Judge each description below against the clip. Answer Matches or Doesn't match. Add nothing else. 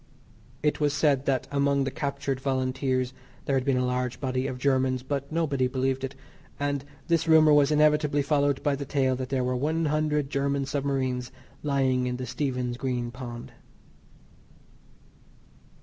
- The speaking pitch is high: Doesn't match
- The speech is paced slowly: Doesn't match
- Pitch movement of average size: Doesn't match